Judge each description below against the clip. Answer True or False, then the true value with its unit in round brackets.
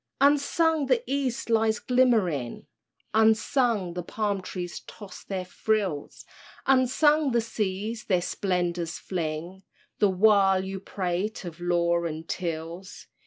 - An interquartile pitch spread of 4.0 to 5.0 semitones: True (4.6 semitones)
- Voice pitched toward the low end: False (195 Hz)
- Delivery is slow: True (120 wpm)